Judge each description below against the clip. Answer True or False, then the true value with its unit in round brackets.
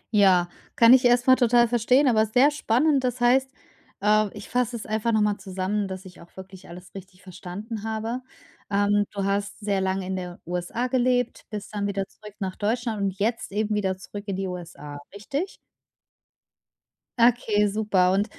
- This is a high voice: True (210 Hz)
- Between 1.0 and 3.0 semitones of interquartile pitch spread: False (3.8 semitones)